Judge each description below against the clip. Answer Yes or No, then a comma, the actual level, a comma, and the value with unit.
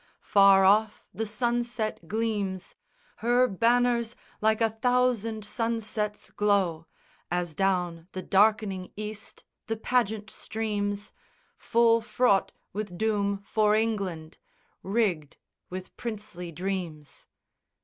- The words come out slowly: Yes, slow, 100 wpm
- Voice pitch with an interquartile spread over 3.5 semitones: No, average, 2.8 semitones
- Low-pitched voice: No, high, 210 Hz